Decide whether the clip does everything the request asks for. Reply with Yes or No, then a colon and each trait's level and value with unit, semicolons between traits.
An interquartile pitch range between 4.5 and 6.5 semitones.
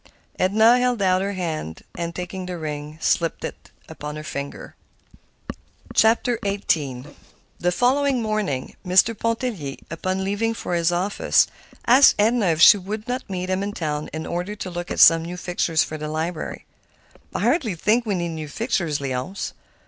Yes: average, 5.1 semitones